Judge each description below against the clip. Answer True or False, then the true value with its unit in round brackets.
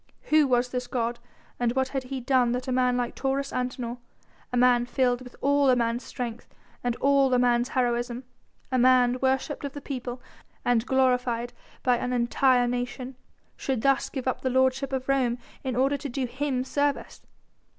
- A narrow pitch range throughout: True (1.5 semitones)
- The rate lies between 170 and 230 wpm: True (180 wpm)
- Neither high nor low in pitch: False (255 Hz)